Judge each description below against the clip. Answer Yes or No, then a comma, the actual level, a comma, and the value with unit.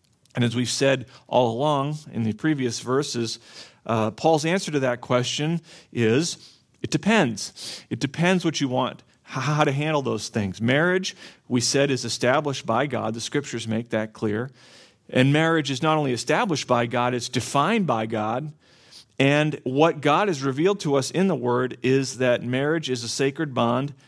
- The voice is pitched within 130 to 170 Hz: Yes, low, 135 Hz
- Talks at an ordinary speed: Yes, average, 175 wpm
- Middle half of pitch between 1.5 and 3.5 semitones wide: No, average, 3.9 semitones